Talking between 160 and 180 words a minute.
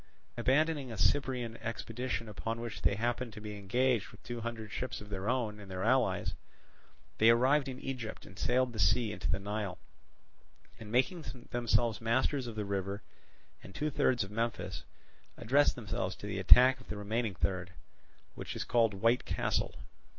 Yes: average, 175 wpm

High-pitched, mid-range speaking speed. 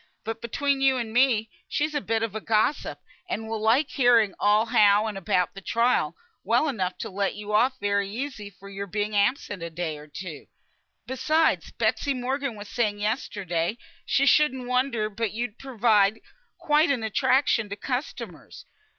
Yes: high, 225 Hz; average, 170 wpm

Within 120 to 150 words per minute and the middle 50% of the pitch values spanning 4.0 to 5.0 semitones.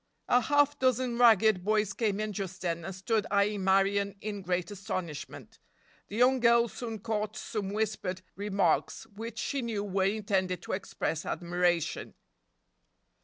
No: average, 145 wpm; average, 3.0 semitones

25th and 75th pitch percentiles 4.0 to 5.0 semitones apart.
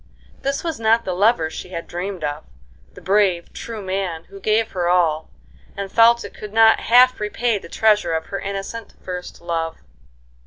Yes: average, 4.3 semitones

